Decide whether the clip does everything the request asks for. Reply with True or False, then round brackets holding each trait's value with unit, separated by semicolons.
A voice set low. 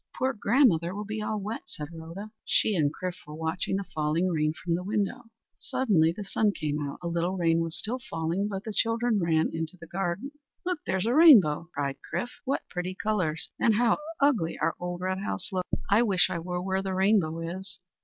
False (185 Hz)